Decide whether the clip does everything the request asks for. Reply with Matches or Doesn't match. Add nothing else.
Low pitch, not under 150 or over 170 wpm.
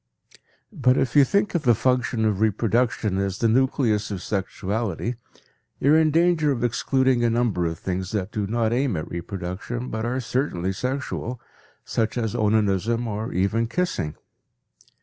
Matches